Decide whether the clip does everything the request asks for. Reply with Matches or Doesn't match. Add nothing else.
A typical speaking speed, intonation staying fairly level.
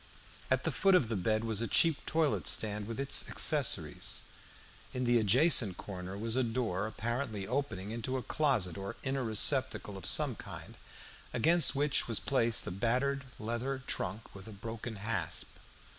Doesn't match